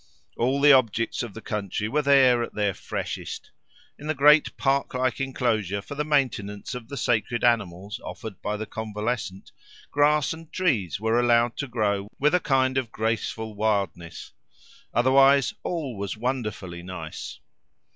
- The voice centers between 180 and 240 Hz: No, low, 120 Hz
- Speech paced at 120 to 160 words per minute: Yes, average, 155 wpm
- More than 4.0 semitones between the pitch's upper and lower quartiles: Yes, average, 4.7 semitones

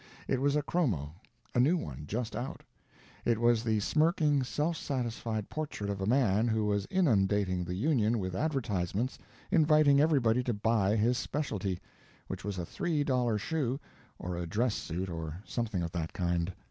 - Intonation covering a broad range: Yes, wide, 6.5 semitones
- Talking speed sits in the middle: Yes, average, 170 wpm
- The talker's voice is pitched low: Yes, low, 115 Hz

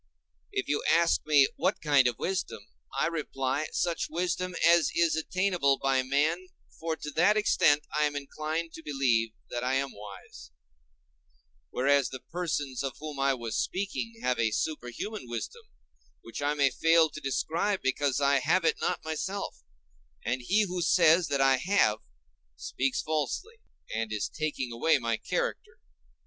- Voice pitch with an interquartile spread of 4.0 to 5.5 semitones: Yes, average, 4.3 semitones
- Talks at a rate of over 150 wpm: Yes, average, 160 wpm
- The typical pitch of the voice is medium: Yes, medium, 150 Hz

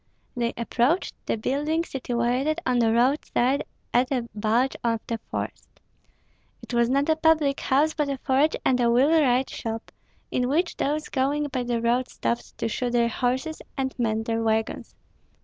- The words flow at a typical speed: Yes, average, 165 wpm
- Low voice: No, very high, 255 Hz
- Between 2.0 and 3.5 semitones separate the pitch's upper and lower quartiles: Yes, average, 3.2 semitones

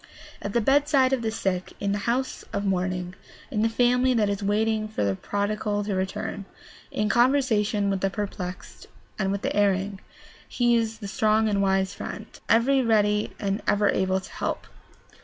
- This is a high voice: Yes, high, 210 Hz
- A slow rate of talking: No, average, 175 wpm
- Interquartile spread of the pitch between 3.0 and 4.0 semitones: No, narrow, 2.5 semitones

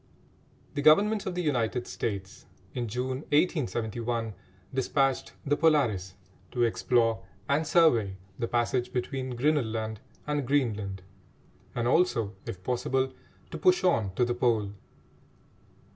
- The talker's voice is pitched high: No, low, 125 Hz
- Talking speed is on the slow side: Yes, slow, 125 wpm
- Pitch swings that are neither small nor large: Yes, average, 4.3 semitones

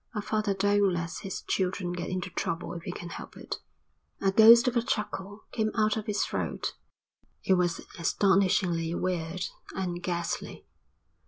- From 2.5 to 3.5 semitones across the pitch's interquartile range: Yes, average, 3.0 semitones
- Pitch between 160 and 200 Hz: Yes, high, 190 Hz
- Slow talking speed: No, average, 160 wpm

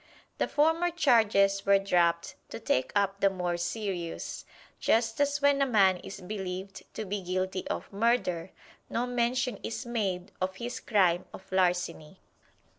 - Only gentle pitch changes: No, average, 4.3 semitones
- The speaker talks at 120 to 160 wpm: Yes, average, 150 wpm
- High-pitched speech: Yes, high, 195 Hz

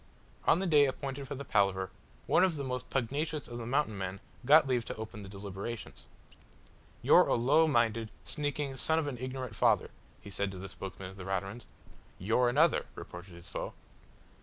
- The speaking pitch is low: Yes, low, 120 Hz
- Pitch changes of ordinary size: No, wide, 6.3 semitones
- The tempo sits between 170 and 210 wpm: Yes, average, 185 wpm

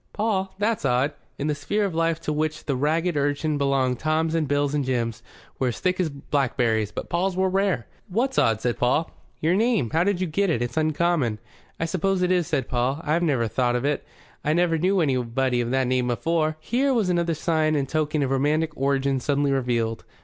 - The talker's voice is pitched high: No, medium, 150 Hz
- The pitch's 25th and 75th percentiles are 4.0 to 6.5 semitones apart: Yes, average, 4.7 semitones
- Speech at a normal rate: No, fast, 210 wpm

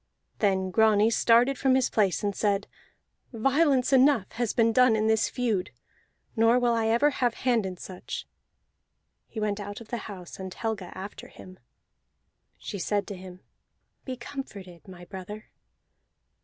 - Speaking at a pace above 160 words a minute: No, average, 155 wpm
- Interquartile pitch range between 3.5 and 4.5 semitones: Yes, average, 3.8 semitones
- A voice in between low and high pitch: No, high, 220 Hz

